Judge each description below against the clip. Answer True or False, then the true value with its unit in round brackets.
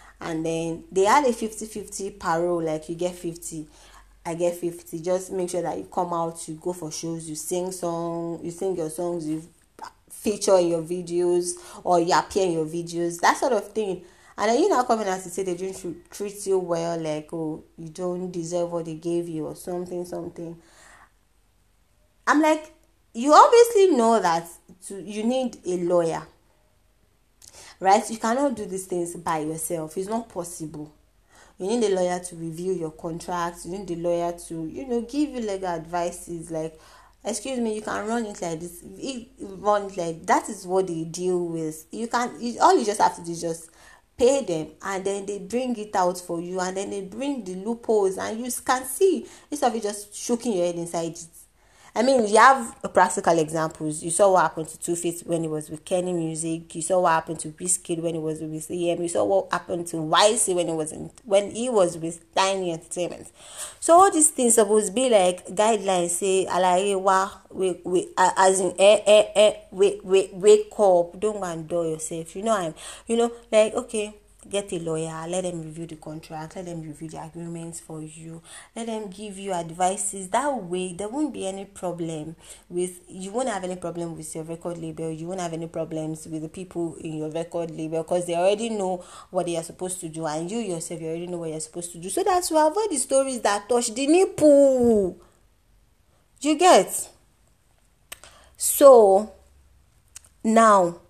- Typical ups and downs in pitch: True (3.8 semitones)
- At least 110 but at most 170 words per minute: False (200 wpm)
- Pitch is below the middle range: False (180 Hz)